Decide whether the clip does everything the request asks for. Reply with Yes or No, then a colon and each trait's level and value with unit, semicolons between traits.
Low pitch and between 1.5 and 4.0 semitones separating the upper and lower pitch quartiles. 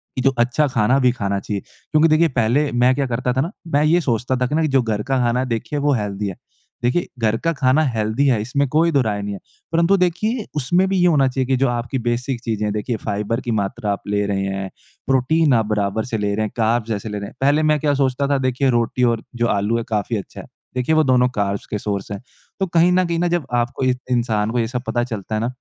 No: low, 125 Hz; average, 4.7 semitones